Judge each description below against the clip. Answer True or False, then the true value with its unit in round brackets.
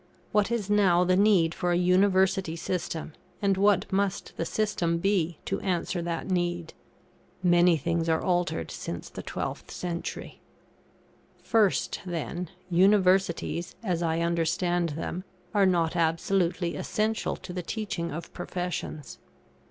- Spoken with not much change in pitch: True (2.2 semitones)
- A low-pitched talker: False (175 Hz)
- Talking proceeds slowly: True (130 wpm)